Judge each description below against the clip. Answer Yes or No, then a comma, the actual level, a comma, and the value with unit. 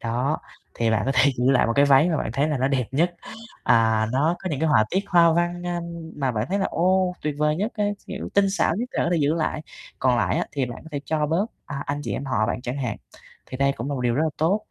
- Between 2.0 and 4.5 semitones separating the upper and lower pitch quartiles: No, average, 5.2 semitones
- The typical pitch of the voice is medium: Yes, medium, 145 Hz